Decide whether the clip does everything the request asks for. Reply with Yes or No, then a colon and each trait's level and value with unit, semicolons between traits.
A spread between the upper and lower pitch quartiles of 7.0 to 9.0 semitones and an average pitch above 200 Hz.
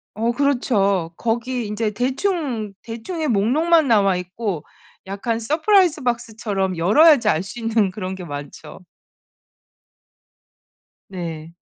No: average, 5.1 semitones; high, 225 Hz